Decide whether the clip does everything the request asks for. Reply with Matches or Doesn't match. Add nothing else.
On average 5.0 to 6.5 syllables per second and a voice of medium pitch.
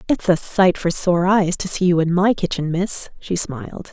Doesn't match